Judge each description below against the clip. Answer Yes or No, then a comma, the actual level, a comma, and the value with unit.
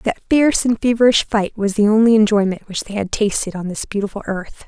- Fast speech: Yes, fast, 220 wpm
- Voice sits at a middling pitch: No, high, 210 Hz